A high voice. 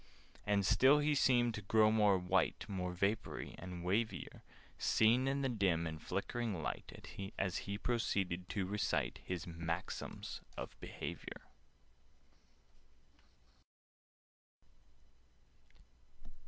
No: low, 100 Hz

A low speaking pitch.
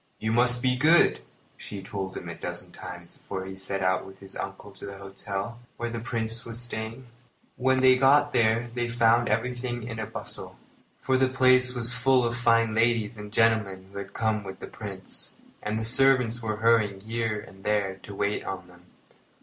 Yes: low, 115 Hz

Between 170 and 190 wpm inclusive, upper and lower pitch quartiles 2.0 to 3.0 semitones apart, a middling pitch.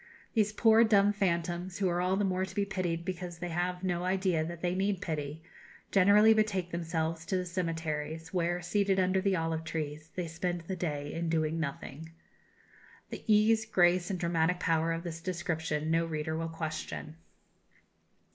Yes: average, 175 wpm; narrow, 2.6 semitones; medium, 175 Hz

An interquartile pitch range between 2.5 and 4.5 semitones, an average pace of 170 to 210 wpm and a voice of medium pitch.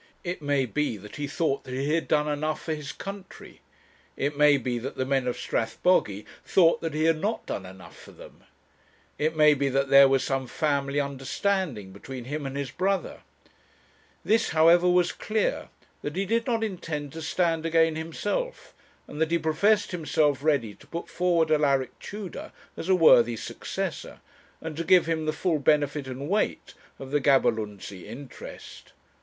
Yes: average, 3.7 semitones; average, 175 wpm; medium, 150 Hz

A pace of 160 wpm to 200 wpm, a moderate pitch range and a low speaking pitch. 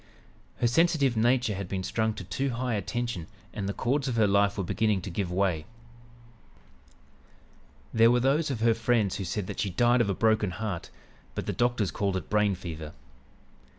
Yes: average, 190 wpm; average, 3.8 semitones; low, 110 Hz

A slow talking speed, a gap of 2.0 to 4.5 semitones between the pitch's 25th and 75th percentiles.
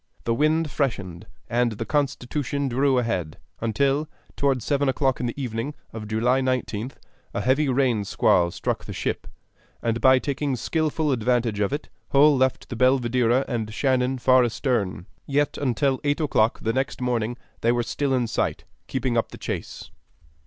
No: average, 165 wpm; average, 3.1 semitones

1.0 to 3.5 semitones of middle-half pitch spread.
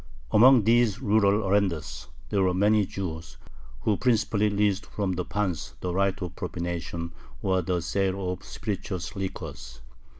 Yes: narrow, 2.5 semitones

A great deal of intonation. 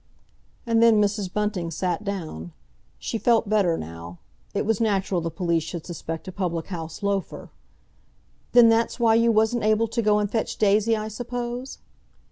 No: average, 4.5 semitones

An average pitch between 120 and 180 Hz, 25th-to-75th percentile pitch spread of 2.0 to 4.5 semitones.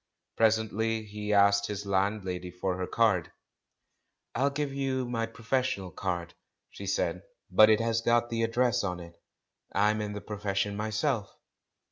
No: low, 105 Hz; narrow, 2.6 semitones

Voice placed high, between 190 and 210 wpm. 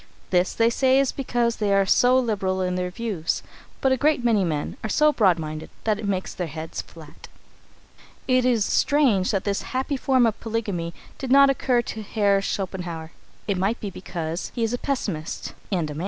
Yes: high, 205 Hz; average, 200 wpm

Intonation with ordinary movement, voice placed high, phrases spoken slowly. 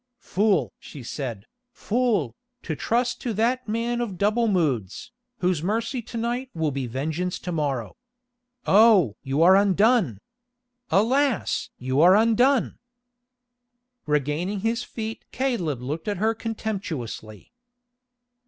No: wide, 7.5 semitones; high, 195 Hz; slow, 120 wpm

